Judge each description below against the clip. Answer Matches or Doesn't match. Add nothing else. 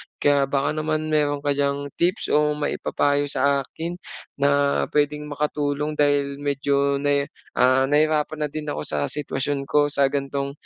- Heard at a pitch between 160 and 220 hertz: Doesn't match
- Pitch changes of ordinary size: Doesn't match